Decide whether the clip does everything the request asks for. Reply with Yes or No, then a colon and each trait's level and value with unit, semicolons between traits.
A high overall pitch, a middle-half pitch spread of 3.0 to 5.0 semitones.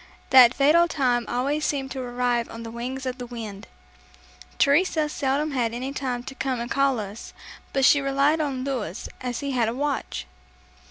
No: very high, 260 Hz; narrow, 2.5 semitones